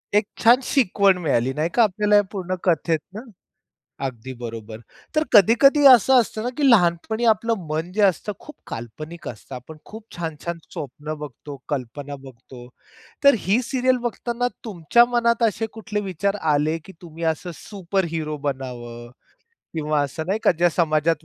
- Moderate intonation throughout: No, wide, 6.7 semitones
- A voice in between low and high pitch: Yes, medium, 170 Hz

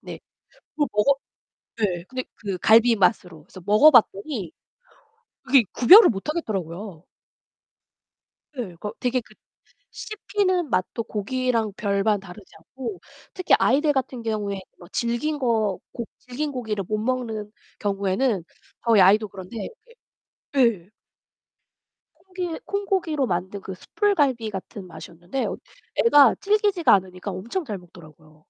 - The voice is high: Yes, high, 220 Hz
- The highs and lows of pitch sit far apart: Yes, wide, 6.0 semitones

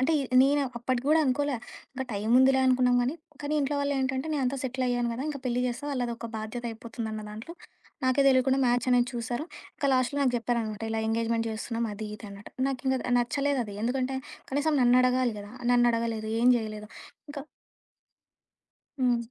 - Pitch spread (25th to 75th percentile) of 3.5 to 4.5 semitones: No, narrow, 2.4 semitones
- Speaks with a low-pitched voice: No, high, 245 Hz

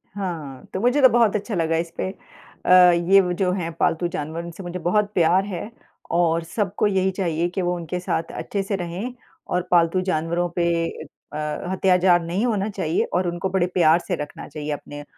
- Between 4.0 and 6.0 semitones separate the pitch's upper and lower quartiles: No, narrow, 2.4 semitones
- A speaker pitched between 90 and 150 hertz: No, medium, 180 Hz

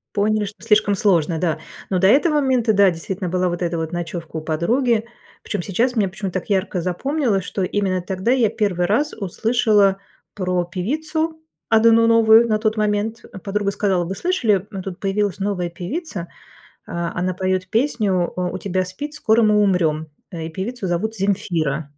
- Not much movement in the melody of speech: No, average, 3.7 semitones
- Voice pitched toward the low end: No, high, 195 Hz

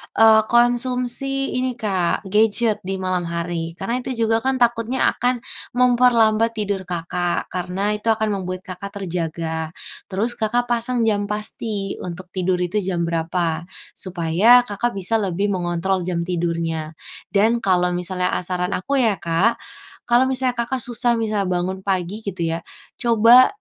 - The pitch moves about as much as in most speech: Yes, average, 4.7 semitones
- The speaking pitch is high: Yes, high, 200 Hz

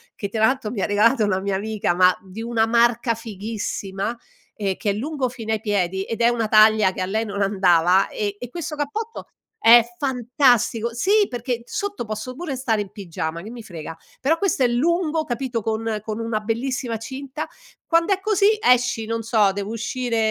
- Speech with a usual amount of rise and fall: Yes, average, 3.6 semitones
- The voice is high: Yes, high, 225 Hz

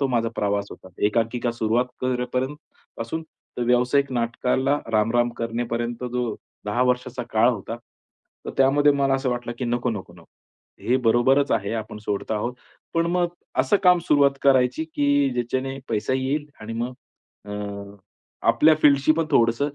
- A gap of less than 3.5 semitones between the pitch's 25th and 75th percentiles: Yes, average, 3.0 semitones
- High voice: No, low, 125 Hz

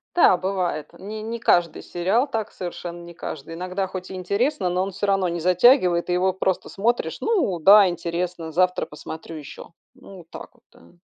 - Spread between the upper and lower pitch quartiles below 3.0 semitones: Yes, narrow, 2.6 semitones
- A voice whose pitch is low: No, medium, 185 Hz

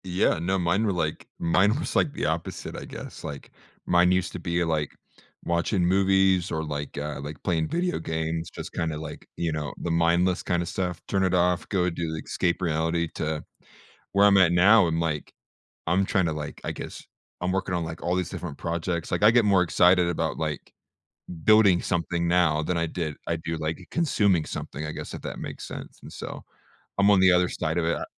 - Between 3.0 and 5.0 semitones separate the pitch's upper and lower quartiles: No, narrow, 2.4 semitones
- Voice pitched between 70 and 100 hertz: Yes, very low, 85 Hz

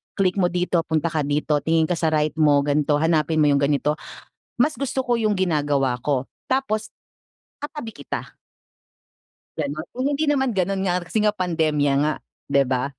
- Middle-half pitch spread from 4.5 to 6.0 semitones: Yes, wide, 5.4 semitones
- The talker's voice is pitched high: No, medium, 160 Hz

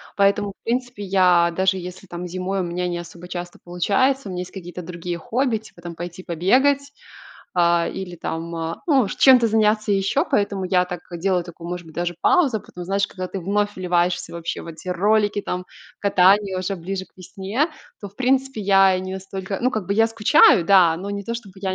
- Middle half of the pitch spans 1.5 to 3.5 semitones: Yes, average, 2.8 semitones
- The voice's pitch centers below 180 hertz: No, high, 190 Hz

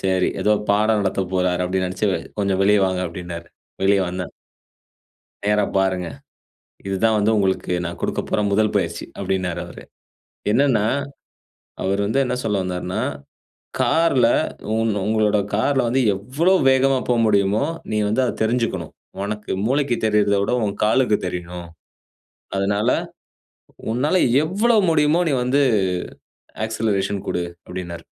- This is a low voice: Yes, low, 105 Hz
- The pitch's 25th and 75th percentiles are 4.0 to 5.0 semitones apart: Yes, average, 4.4 semitones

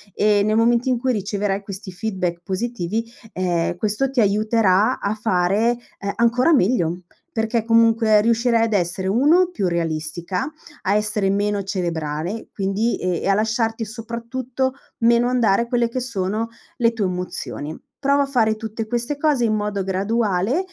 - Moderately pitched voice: No, high, 215 Hz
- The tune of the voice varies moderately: Yes, average, 3.4 semitones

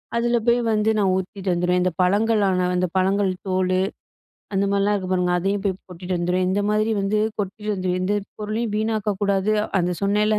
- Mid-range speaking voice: No, high, 195 Hz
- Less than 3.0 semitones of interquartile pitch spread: Yes, narrow, 2.4 semitones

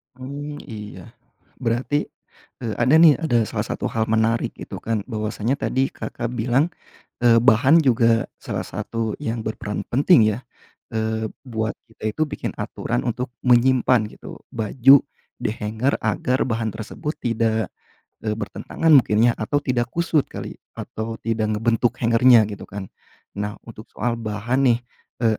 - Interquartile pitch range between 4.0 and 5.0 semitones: No, average, 2.7 semitones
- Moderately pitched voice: No, low, 115 Hz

